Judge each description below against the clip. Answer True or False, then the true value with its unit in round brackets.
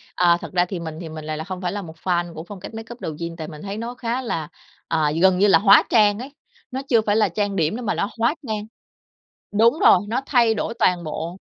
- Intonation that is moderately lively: True (4.9 semitones)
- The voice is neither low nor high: False (195 Hz)